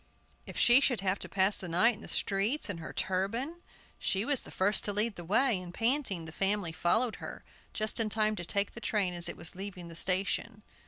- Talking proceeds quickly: Yes, fast, 225 wpm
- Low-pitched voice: No, high, 200 Hz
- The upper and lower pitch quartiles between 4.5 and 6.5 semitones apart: No, average, 3.8 semitones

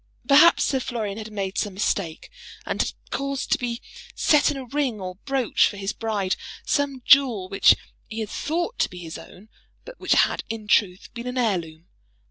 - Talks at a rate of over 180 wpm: Yes, average, 190 wpm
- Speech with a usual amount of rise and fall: No, wide, 5.7 semitones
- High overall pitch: Yes, high, 225 Hz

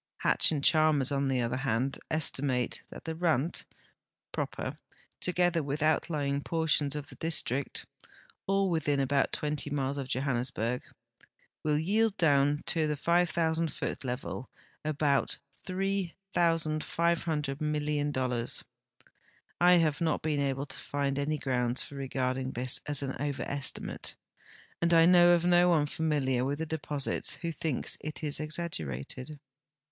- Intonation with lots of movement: No, average, 3.2 semitones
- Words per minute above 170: No, slow, 135 wpm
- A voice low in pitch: No, medium, 150 Hz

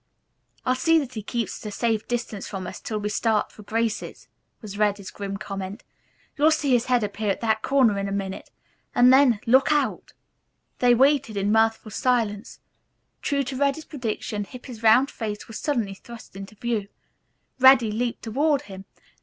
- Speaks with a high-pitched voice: Yes, high, 225 Hz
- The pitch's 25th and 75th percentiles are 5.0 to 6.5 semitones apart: No, average, 3.6 semitones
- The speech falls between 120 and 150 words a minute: No, average, 175 wpm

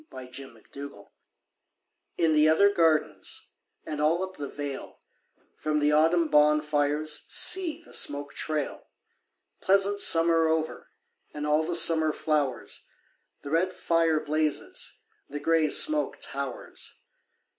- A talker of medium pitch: Yes, medium, 155 Hz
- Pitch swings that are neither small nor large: No, narrow, 2.1 semitones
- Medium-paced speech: No, slow, 125 wpm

